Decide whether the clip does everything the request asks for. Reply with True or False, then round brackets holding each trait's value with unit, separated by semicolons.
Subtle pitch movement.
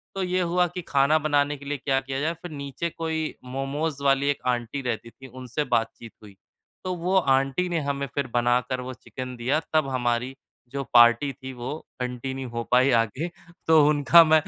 False (3.6 semitones)